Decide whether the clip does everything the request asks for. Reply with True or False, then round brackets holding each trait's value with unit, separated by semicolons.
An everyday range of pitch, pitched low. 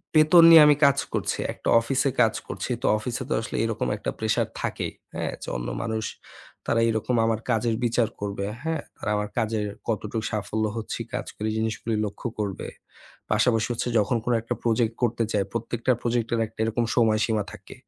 False (1.9 semitones; 115 Hz)